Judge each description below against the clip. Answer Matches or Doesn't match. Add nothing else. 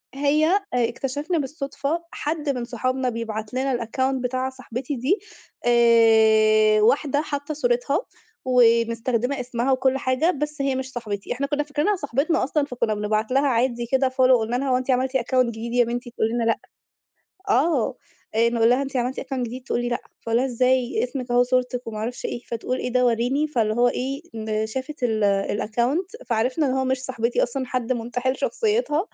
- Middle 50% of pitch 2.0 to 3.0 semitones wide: Matches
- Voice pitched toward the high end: Matches